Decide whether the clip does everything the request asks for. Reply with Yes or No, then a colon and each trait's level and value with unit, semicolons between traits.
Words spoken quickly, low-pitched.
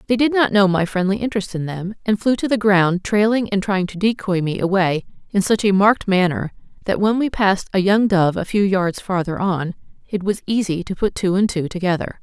No: fast, 230 wpm; high, 195 Hz